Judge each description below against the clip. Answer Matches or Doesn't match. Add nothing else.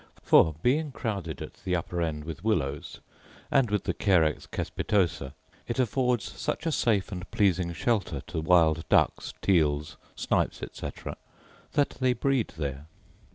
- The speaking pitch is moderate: Doesn't match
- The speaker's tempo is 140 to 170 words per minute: Matches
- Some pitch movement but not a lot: Doesn't match